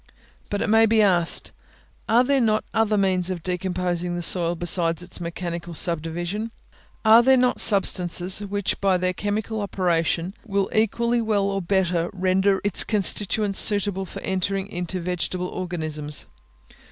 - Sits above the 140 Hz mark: Yes, high, 190 Hz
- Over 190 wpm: No, average, 145 wpm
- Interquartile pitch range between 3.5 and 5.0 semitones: No, average, 2.9 semitones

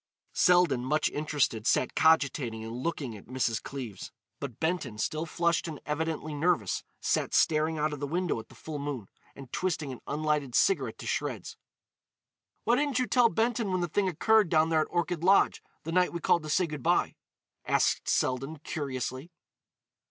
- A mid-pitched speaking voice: Yes, medium, 155 Hz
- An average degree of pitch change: Yes, average, 4.4 semitones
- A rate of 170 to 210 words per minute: Yes, average, 175 wpm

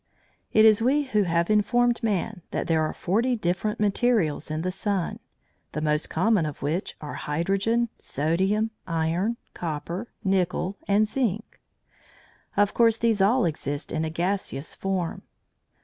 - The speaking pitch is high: Yes, high, 195 Hz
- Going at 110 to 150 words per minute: Yes, average, 145 wpm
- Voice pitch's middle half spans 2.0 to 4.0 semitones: No, average, 4.9 semitones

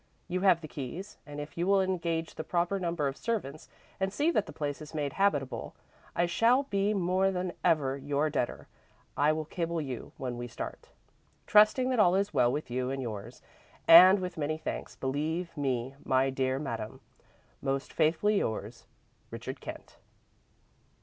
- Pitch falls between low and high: Yes, medium, 160 Hz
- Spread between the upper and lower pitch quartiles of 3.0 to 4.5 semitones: No, wide, 5.5 semitones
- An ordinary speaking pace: Yes, average, 170 wpm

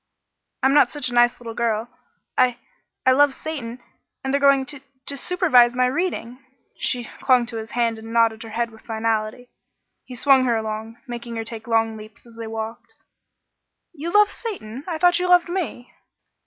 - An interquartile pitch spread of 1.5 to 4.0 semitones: Yes, average, 3.6 semitones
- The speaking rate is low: No, average, 180 wpm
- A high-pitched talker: Yes, high, 240 Hz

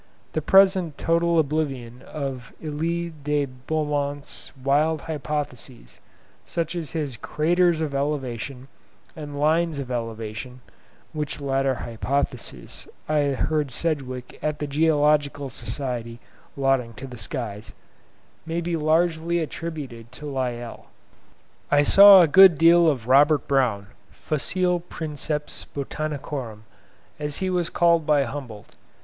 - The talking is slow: Yes, slow, 120 wpm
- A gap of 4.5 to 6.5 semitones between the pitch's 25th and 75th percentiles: No, average, 3.7 semitones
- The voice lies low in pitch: No, medium, 145 Hz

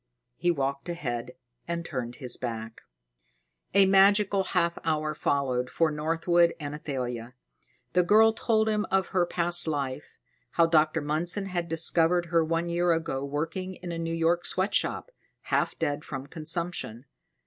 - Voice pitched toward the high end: No, medium, 165 Hz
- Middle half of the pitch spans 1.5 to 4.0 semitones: Yes, average, 3.5 semitones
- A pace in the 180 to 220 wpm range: No, average, 150 wpm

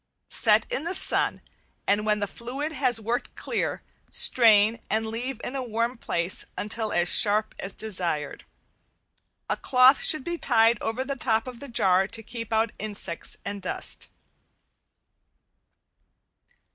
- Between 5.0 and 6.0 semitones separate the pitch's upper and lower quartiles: No, average, 3.4 semitones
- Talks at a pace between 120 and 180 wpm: Yes, average, 145 wpm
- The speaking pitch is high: Yes, high, 225 Hz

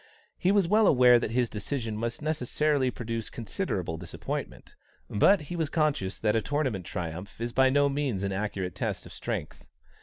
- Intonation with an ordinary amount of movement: No, wide, 6.2 semitones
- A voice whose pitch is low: Yes, low, 120 Hz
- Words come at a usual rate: Yes, average, 175 wpm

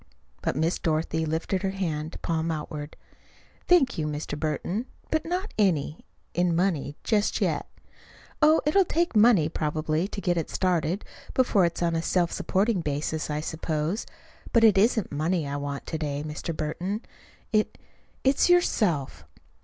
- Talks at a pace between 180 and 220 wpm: No, average, 155 wpm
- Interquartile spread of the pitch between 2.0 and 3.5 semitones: No, average, 5.2 semitones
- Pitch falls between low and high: Yes, medium, 170 Hz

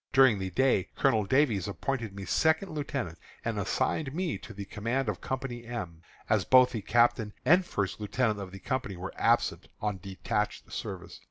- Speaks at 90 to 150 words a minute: No, average, 175 wpm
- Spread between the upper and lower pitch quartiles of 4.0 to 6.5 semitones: Yes, average, 5.1 semitones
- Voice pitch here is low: Yes, low, 115 Hz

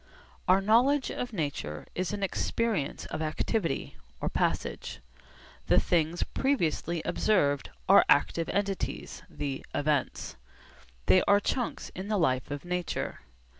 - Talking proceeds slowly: Yes, slow, 125 wpm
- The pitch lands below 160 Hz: No, medium, 175 Hz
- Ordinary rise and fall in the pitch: No, wide, 6.1 semitones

